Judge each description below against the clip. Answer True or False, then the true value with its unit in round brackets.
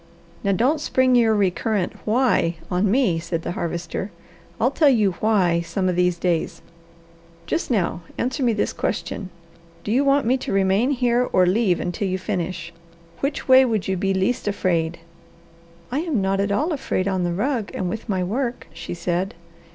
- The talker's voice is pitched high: True (200 Hz)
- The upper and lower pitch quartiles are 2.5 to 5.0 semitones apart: False (5.6 semitones)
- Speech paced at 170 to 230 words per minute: True (180 wpm)